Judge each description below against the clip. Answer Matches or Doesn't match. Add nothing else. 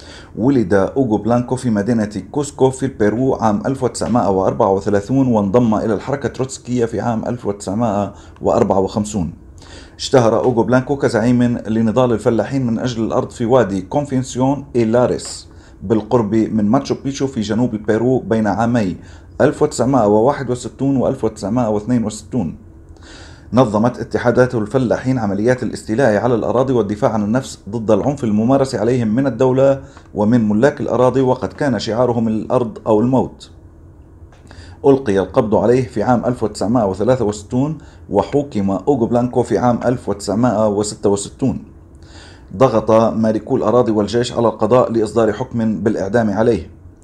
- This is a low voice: Matches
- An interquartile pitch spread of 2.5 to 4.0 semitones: Matches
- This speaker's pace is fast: Doesn't match